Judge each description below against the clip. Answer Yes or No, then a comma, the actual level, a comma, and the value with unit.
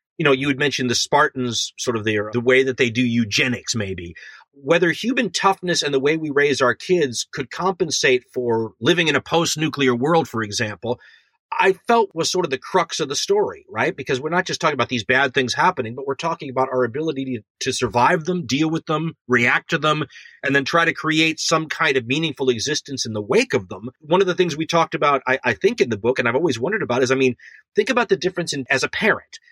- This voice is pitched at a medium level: Yes, medium, 145 Hz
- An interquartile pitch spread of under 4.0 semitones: No, average, 4.8 semitones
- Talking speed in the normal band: No, fast, 245 wpm